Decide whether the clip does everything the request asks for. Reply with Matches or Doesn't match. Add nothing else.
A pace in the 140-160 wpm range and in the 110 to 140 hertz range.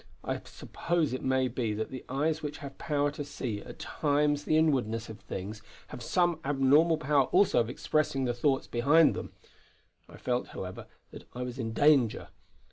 Doesn't match